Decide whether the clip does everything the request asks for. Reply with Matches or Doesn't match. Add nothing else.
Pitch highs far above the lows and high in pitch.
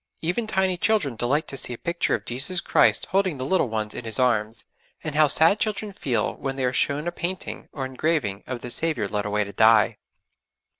Doesn't match